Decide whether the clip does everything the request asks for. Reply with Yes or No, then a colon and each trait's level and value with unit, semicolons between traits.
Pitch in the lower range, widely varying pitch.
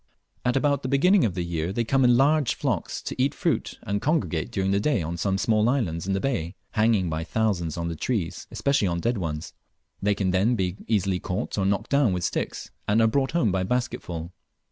Yes: low, 100 Hz; wide, 5.9 semitones